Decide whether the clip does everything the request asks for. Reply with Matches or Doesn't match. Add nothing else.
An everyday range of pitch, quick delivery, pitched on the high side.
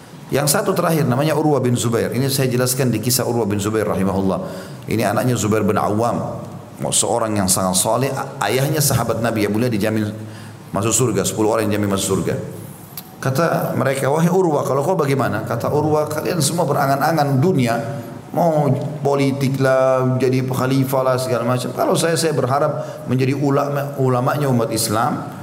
Doesn't match